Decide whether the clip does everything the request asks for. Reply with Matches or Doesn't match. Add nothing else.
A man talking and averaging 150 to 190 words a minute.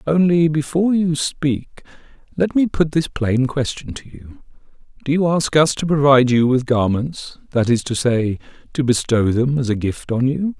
Matches